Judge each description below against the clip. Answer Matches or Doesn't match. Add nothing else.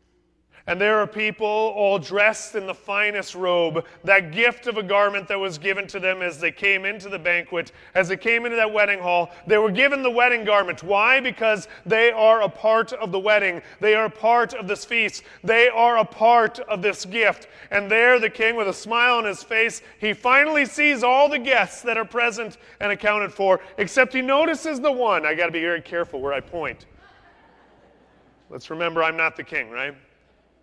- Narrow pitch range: Doesn't match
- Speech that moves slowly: Doesn't match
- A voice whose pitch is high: Matches